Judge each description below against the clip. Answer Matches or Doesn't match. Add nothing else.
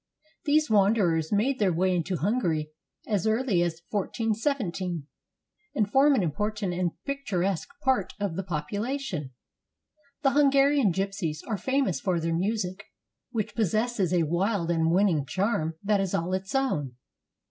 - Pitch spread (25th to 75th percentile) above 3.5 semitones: Matches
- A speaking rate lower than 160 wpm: Matches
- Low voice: Doesn't match